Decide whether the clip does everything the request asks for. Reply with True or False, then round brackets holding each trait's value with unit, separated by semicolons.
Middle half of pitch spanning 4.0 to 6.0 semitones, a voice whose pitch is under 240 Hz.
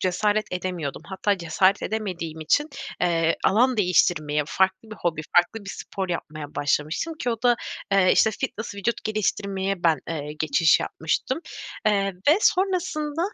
True (4.7 semitones; 190 Hz)